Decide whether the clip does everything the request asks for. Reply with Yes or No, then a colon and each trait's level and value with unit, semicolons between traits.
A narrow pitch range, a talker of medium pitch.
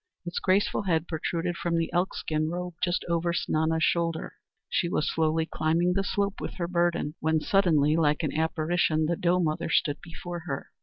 Yes: narrow, 1.8 semitones; medium, 170 Hz